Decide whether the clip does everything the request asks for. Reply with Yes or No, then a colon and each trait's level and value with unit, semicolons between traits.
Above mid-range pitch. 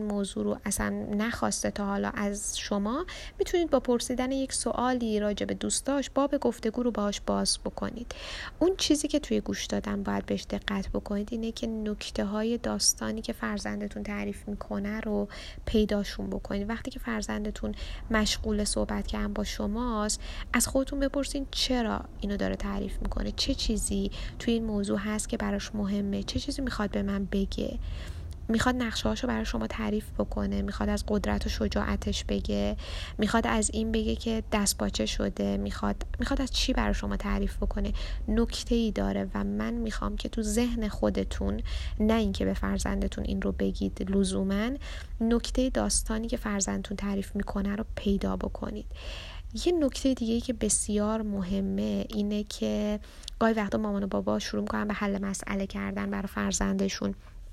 Yes: high, 200 Hz